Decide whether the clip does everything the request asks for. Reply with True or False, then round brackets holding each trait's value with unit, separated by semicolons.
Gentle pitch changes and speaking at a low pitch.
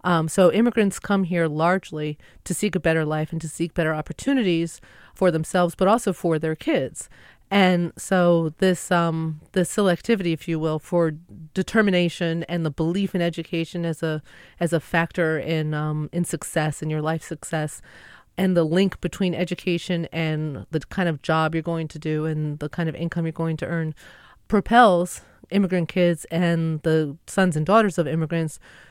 False (2.2 semitones; 170 Hz)